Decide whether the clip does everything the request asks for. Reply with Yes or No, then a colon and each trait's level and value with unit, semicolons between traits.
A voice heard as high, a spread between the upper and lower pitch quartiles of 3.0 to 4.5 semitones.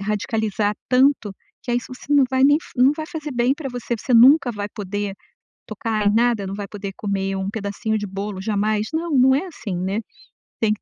Yes: high, 220 Hz; average, 4.0 semitones